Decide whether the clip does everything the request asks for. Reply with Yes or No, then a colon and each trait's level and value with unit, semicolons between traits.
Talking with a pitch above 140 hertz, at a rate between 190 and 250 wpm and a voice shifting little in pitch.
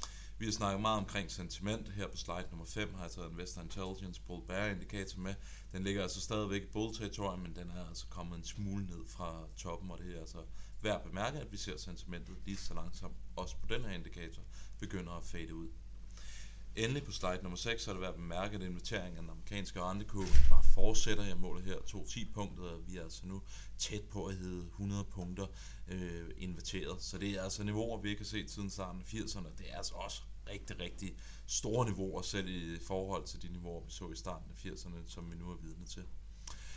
No: very low, 95 Hz; average, 220 wpm; narrow, 2.3 semitones